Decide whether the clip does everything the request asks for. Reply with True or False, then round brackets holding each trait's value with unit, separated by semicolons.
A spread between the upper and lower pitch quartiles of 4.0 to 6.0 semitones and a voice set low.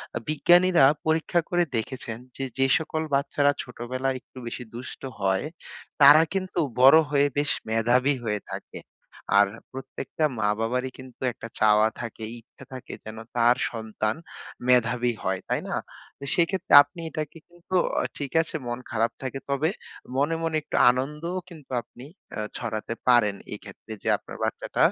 True (4.7 semitones; 130 Hz)